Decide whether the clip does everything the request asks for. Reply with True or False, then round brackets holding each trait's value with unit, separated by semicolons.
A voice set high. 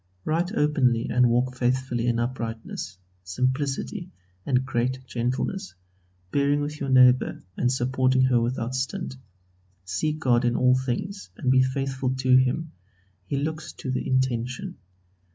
False (130 Hz)